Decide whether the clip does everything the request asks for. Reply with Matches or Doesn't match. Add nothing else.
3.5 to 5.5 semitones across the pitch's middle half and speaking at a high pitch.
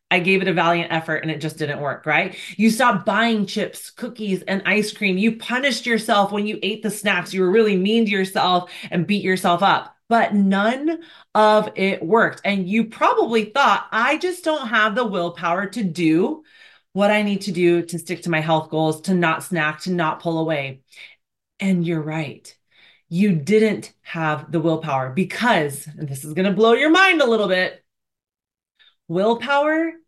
Matches